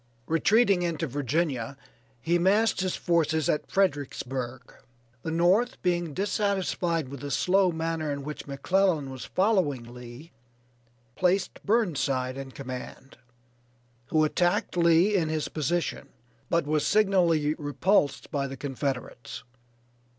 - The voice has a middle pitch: Yes, medium, 160 Hz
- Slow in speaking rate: Yes, slow, 120 wpm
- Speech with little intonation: No, average, 4.8 semitones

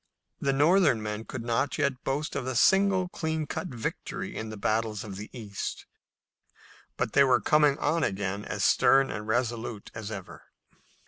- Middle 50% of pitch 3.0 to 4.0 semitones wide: No, average, 5.1 semitones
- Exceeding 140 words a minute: Yes, average, 170 wpm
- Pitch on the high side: No, low, 120 Hz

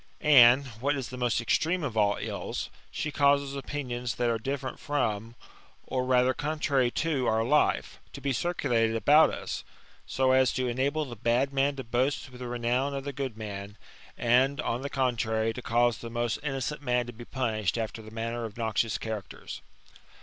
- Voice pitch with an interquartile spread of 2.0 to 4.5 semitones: Yes, average, 3.2 semitones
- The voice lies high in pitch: No, low, 125 Hz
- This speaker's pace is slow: No, average, 185 wpm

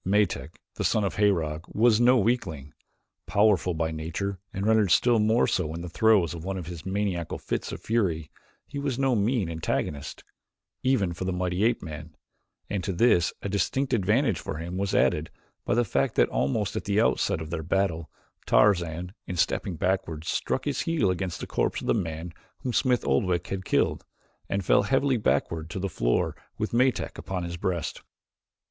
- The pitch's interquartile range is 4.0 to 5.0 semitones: Yes, average, 4.7 semitones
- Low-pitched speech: Yes, very low, 95 Hz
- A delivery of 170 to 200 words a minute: Yes, average, 185 wpm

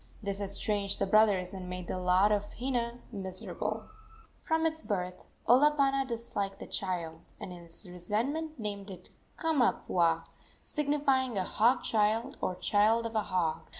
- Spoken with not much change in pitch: No, average, 5.1 semitones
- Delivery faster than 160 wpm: No, average, 150 wpm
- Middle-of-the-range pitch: No, high, 210 Hz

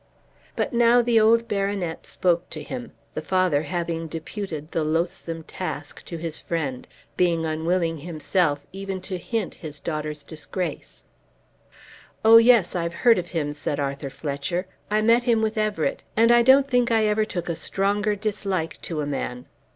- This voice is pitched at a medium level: Yes, medium, 180 Hz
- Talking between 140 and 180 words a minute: Yes, average, 165 wpm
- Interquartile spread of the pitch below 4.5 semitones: No, average, 5.3 semitones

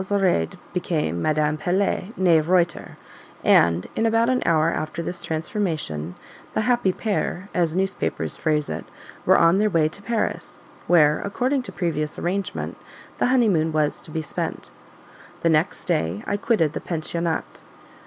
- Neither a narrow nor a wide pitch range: Yes, average, 4.4 semitones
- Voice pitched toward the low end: No, medium, 170 Hz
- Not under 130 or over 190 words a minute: Yes, average, 150 wpm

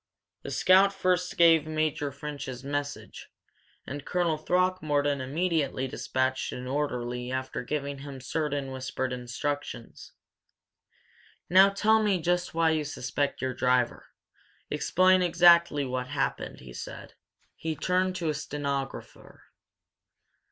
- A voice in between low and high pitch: Yes, medium, 145 Hz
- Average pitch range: Yes, average, 4.6 semitones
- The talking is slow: Yes, slow, 115 wpm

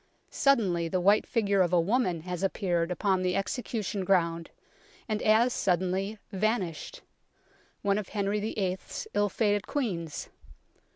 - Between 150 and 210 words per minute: No, slow, 135 wpm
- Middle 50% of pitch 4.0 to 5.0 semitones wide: No, average, 3.0 semitones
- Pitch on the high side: Yes, high, 195 Hz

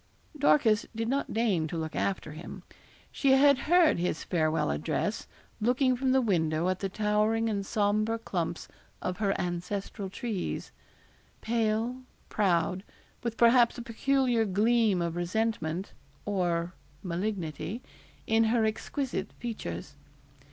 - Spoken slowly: Yes, slow, 125 wpm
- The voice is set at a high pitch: Yes, high, 210 Hz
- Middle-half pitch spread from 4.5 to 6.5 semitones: Yes, average, 4.8 semitones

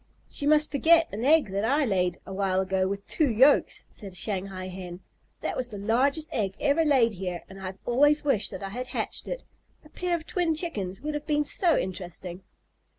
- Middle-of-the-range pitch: No, high, 225 Hz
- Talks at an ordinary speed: No, fast, 215 wpm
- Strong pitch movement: Yes, wide, 7.7 semitones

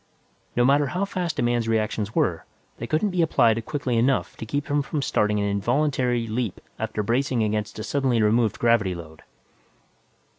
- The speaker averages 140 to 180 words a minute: Yes, average, 175 wpm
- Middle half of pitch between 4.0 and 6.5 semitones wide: Yes, average, 4.4 semitones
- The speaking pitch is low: Yes, low, 120 Hz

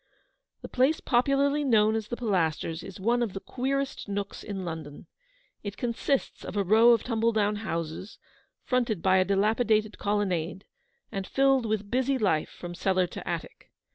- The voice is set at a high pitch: Yes, high, 210 Hz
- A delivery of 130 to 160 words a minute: No, average, 170 wpm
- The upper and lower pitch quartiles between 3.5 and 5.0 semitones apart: Yes, average, 4.2 semitones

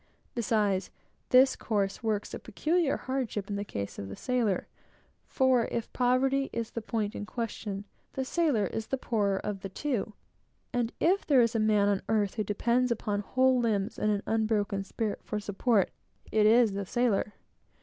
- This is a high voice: Yes, high, 220 Hz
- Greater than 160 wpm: Yes, average, 175 wpm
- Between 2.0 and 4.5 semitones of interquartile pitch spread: Yes, average, 3.5 semitones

